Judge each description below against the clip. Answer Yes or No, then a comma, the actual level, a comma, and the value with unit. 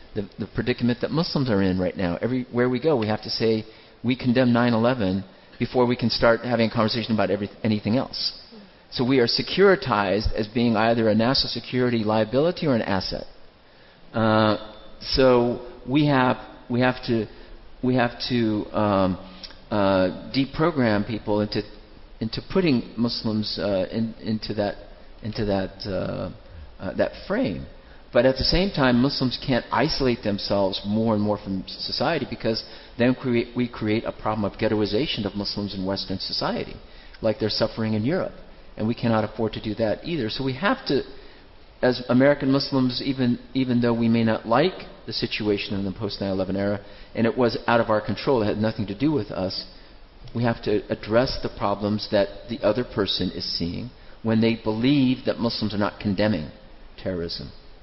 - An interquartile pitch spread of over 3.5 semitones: No, average, 3.1 semitones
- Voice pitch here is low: Yes, low, 110 Hz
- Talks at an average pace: Yes, average, 175 wpm